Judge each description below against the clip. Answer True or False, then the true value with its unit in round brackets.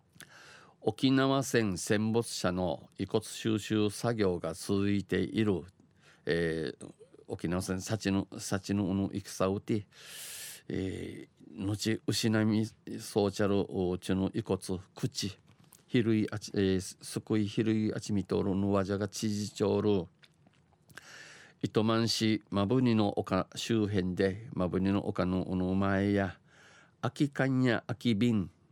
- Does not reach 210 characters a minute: True (190 characters per minute)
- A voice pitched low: True (100 Hz)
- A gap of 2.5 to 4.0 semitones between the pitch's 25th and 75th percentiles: True (2.8 semitones)